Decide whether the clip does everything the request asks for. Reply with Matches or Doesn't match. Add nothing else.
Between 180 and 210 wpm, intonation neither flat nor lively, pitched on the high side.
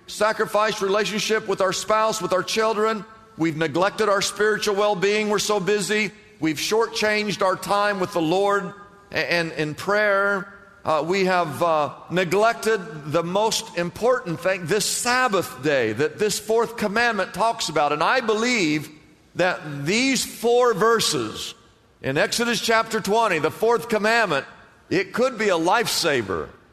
Doesn't match